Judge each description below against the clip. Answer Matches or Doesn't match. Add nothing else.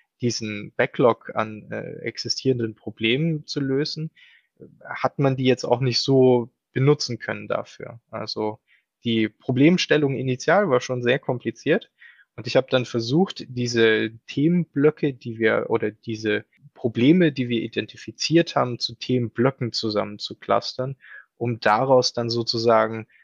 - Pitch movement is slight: Doesn't match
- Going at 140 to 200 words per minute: Doesn't match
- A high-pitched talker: Doesn't match